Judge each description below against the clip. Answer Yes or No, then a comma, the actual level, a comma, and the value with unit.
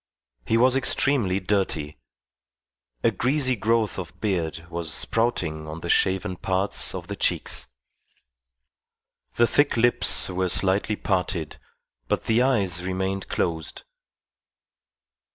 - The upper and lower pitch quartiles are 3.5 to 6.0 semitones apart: Yes, average, 4.7 semitones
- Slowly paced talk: Yes, slow, 115 wpm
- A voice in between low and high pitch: No, very low, 95 Hz